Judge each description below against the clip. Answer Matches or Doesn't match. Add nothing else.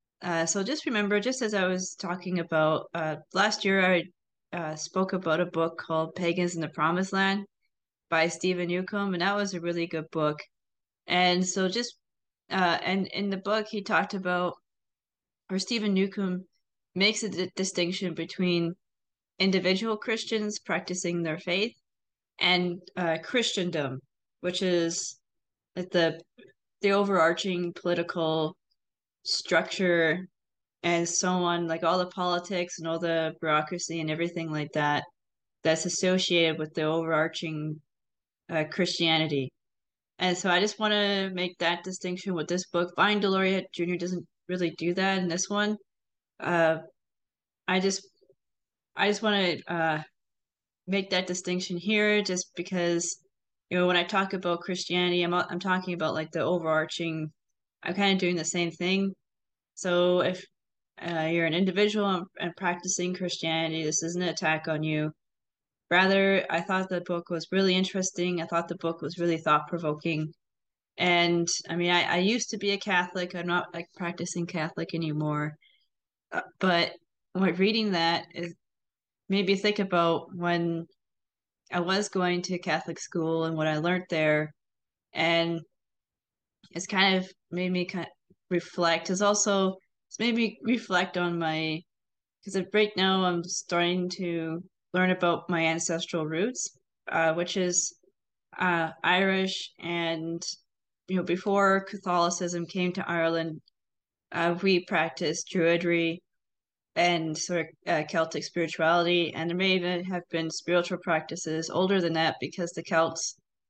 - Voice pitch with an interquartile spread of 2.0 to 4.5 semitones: Matches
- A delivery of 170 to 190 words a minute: Doesn't match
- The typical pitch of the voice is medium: Matches